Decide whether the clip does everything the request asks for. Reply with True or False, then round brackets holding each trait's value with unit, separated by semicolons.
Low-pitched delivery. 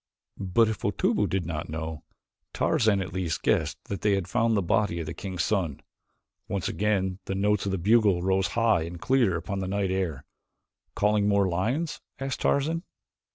True (95 Hz)